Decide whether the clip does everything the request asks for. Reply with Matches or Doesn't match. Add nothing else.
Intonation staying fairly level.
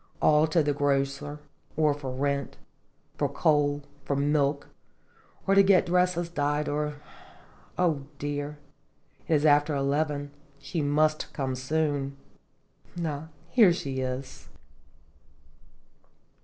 Matches